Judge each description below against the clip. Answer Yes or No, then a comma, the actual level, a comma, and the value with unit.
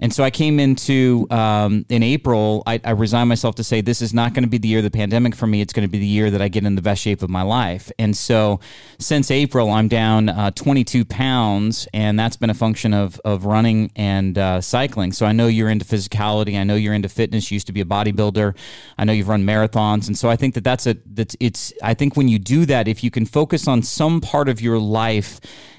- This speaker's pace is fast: Yes, fast, 255 wpm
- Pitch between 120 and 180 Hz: No, low, 110 Hz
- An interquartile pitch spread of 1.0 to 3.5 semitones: Yes, narrow, 2.4 semitones